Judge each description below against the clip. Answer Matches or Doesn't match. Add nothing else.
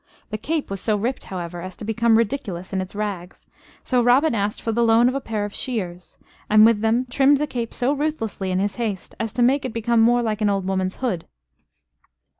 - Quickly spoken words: Matches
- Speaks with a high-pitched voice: Matches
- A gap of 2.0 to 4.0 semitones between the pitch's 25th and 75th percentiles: Matches